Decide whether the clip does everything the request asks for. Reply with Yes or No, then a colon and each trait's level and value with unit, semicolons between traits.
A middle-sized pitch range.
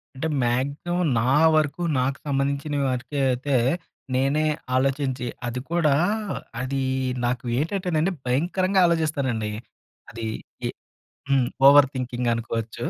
Yes: average, 3.4 semitones